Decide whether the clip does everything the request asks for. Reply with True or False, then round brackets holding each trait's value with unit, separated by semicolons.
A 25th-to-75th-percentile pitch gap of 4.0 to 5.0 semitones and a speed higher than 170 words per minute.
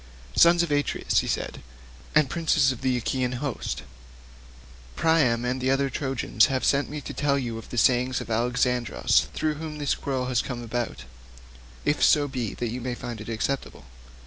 False (3.0 semitones; 180 wpm)